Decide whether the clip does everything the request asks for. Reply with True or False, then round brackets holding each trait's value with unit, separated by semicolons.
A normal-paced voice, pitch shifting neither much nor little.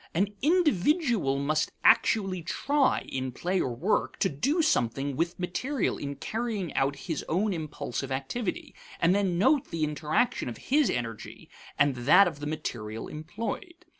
False (150 wpm; 7.9 semitones)